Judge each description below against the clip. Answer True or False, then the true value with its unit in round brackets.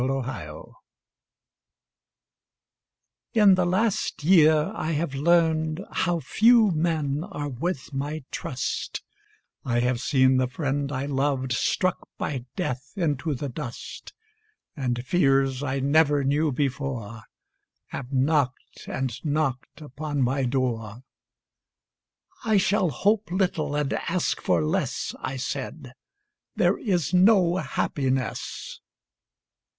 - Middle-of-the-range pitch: True (145 Hz)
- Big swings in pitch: False (4.3 semitones)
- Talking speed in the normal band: False (115 wpm)